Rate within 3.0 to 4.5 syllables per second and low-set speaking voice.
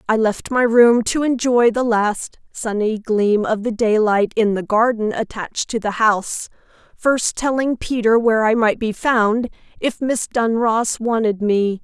No: 4.2 syllables/s; high, 225 Hz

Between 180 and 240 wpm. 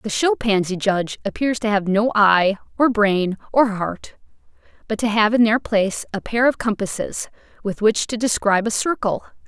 Yes: average, 185 wpm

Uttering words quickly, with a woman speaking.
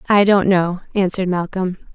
No: average, 155 wpm; female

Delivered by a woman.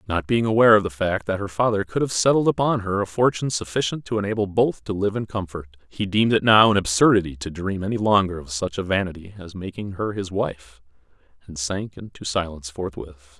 No: male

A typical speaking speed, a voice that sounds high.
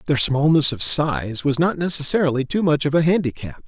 No: average, 195 wpm; medium, 145 Hz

